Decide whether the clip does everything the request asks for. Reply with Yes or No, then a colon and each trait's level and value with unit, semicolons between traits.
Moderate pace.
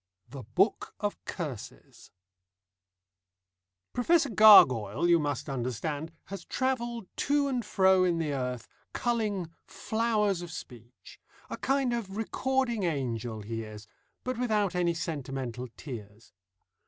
No: slow, 115 wpm